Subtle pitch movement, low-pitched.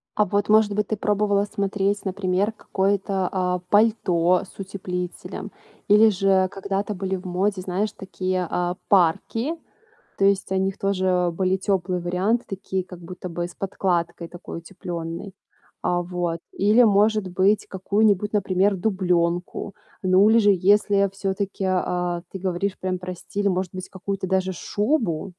No: narrow, 2.0 semitones; high, 190 Hz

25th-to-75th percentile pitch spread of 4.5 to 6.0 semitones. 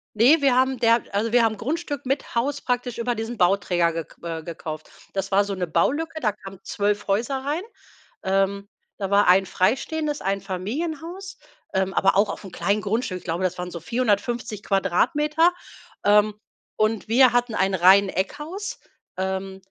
Yes: average, 5.2 semitones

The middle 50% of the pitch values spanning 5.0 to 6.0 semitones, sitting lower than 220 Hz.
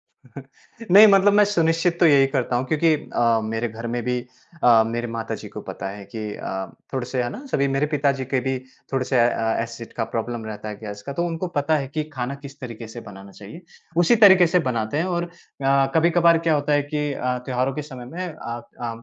Yes: wide, 5.4 semitones; low, 135 Hz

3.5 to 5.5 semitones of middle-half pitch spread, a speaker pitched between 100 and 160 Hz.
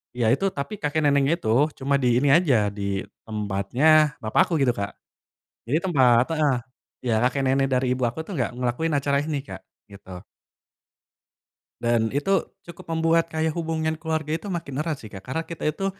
Yes: average, 4.5 semitones; medium, 140 Hz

